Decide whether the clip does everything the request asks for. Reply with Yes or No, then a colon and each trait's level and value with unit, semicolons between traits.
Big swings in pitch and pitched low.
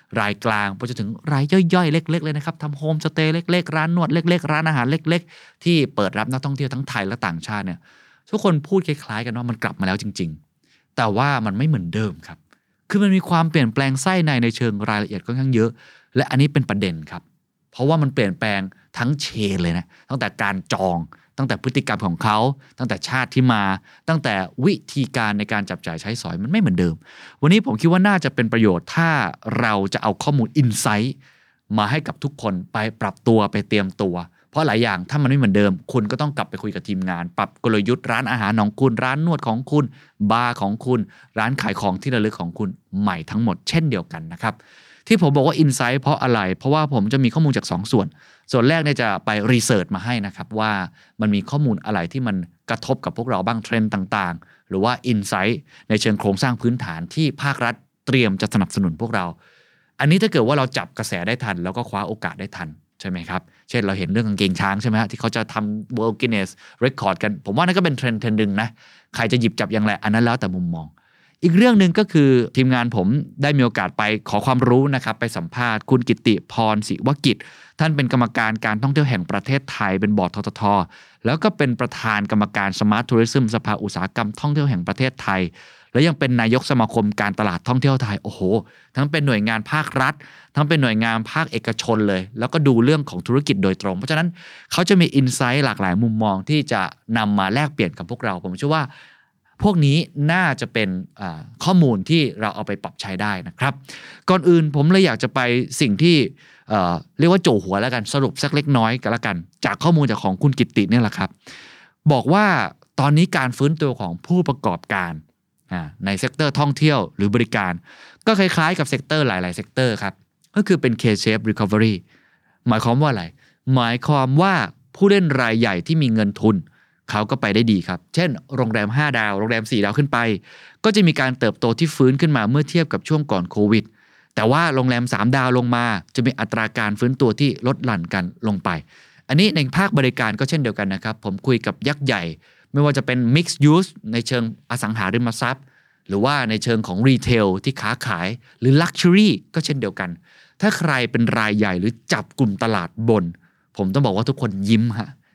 Yes: wide, 5.7 semitones; low, 120 Hz